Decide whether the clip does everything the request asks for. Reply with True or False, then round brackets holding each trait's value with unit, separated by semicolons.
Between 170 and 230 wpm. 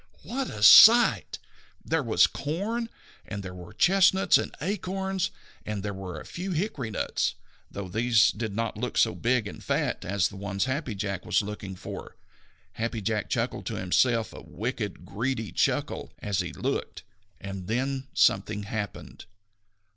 False (155 wpm)